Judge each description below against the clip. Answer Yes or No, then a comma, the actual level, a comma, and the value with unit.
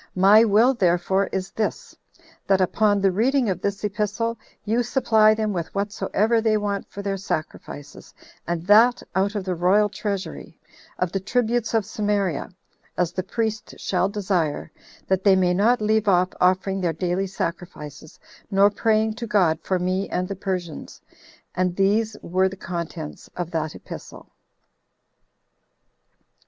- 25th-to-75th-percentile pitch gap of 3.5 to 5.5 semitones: No, average, 2.9 semitones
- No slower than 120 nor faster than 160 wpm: Yes, average, 150 wpm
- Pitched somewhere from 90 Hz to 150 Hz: No, high, 195 Hz